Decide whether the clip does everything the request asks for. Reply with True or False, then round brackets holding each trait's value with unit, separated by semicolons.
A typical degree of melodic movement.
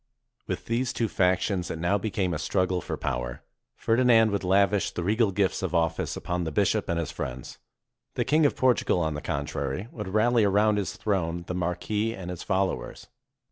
True (3.9 semitones)